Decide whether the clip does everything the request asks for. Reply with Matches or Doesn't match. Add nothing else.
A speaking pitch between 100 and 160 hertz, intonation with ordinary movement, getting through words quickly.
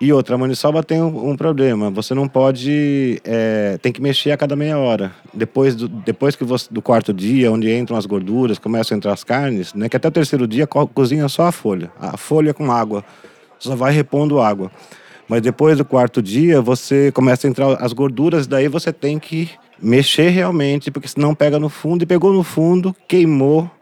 Matches